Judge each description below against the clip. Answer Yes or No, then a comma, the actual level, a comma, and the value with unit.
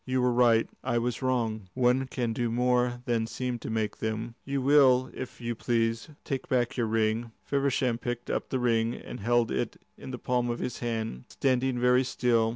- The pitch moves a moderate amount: No, narrow, 1.8 semitones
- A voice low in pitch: Yes, low, 120 Hz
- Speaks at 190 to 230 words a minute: Yes, average, 195 wpm